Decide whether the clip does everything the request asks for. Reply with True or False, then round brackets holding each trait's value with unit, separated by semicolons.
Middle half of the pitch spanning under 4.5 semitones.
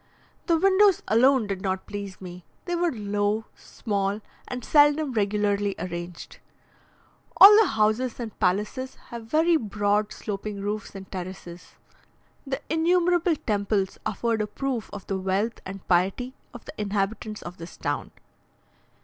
False (4.9 semitones)